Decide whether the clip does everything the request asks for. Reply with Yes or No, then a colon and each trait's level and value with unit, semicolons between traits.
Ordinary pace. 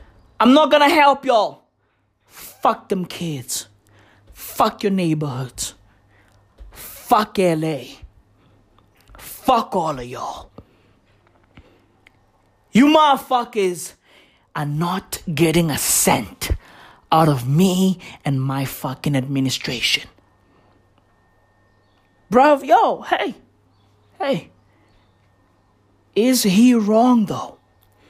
No: slow, 85 wpm